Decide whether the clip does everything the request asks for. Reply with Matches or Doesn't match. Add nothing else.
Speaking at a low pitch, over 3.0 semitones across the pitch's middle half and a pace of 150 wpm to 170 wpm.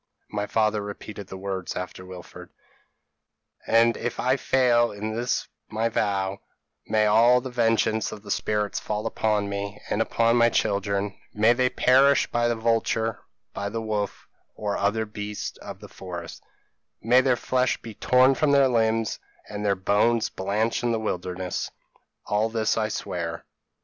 Doesn't match